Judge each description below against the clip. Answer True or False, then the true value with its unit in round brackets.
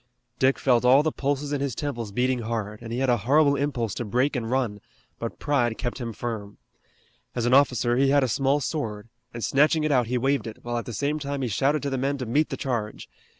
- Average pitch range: True (3.3 semitones)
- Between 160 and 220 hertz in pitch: False (125 Hz)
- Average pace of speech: False (240 wpm)